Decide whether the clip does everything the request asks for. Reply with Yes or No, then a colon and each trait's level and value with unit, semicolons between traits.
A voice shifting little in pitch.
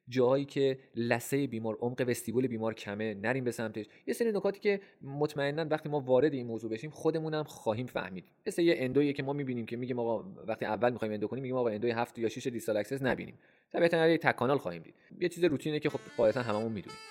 No: average, 5.0 semitones